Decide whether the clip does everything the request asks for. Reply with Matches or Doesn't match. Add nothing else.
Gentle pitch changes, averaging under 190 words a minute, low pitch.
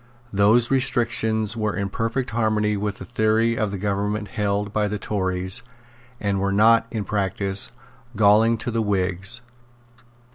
Matches